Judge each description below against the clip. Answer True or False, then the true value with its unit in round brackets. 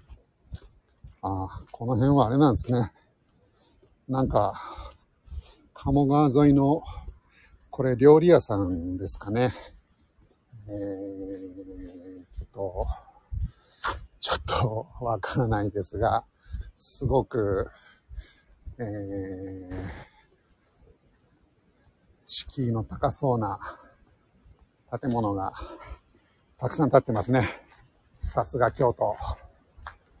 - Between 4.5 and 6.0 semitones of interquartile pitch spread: True (5.6 semitones)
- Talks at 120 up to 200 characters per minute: True (155 characters per minute)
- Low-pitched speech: True (100 Hz)